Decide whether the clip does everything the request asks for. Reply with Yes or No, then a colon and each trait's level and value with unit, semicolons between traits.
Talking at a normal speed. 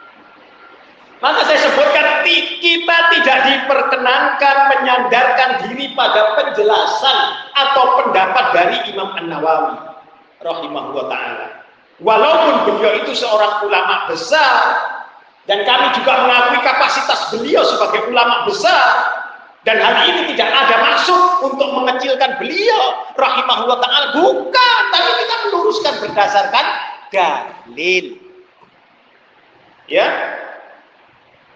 Yes: average, 95 wpm